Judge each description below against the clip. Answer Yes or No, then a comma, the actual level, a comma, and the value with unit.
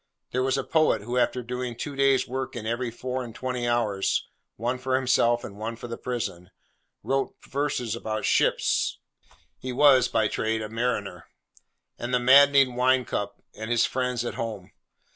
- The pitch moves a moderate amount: No, narrow, 2.2 semitones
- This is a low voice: Yes, low, 125 Hz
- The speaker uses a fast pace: No, average, 175 wpm